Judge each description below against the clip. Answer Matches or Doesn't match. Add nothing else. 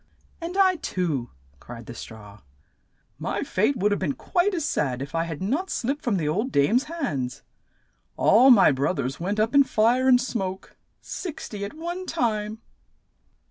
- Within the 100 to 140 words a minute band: Doesn't match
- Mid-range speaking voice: Doesn't match